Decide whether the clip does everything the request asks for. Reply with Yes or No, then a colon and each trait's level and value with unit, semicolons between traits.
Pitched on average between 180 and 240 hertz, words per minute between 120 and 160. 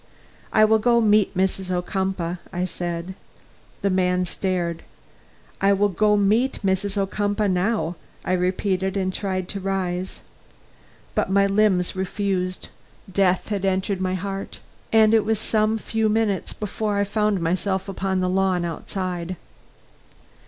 Yes: high, 190 Hz; average, 140 wpm